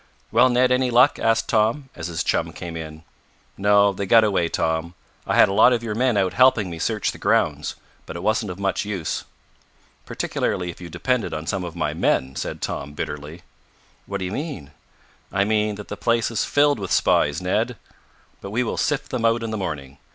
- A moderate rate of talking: No, fast, 210 wpm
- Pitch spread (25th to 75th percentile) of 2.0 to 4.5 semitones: No, average, 5.2 semitones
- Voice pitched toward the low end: Yes, low, 100 Hz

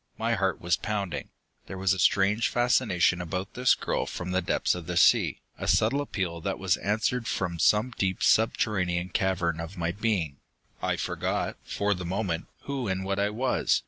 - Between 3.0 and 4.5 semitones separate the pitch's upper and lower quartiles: Yes, average, 3.3 semitones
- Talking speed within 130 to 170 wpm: No, average, 180 wpm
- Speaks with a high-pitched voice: No, very low, 95 Hz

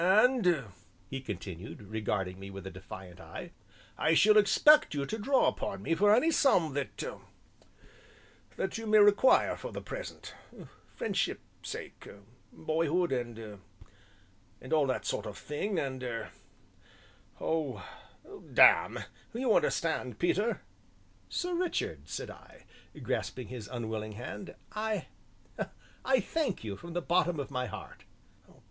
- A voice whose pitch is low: No, medium, 160 Hz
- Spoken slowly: Yes, slow, 130 wpm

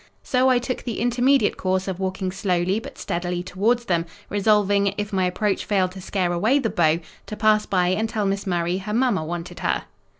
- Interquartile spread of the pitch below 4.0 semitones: Yes, average, 3.1 semitones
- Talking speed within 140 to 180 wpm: No, average, 200 wpm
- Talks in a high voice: Yes, high, 195 Hz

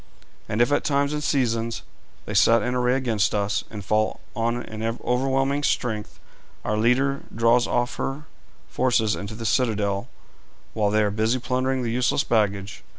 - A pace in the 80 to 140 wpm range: No, average, 160 wpm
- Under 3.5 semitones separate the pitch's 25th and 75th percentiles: Yes, average, 3.1 semitones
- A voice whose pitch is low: Yes, low, 115 Hz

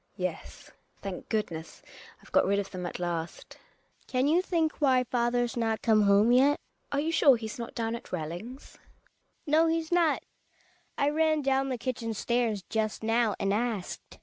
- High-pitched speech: Yes, high, 235 Hz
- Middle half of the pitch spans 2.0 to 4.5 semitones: No, average, 5.0 semitones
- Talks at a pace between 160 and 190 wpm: Yes, average, 180 wpm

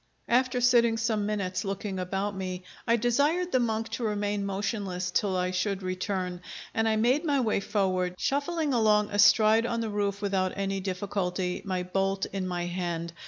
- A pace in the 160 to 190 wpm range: Yes, average, 170 wpm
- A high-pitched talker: Yes, high, 205 Hz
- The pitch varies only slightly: No, average, 3.4 semitones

